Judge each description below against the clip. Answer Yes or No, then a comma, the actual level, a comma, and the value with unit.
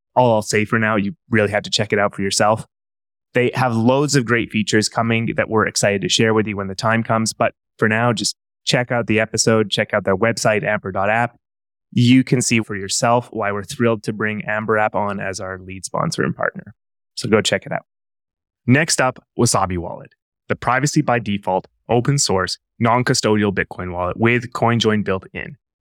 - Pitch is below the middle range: Yes, low, 110 Hz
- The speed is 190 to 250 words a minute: Yes, average, 200 wpm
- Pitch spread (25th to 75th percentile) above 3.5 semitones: No, average, 2.9 semitones